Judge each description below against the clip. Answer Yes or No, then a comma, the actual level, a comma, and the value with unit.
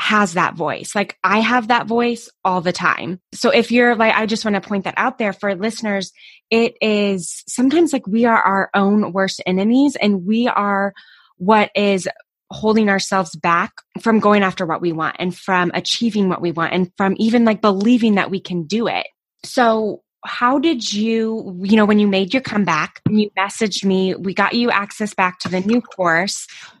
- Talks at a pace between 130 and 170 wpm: No, average, 200 wpm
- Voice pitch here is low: No, high, 205 Hz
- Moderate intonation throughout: Yes, average, 3.0 semitones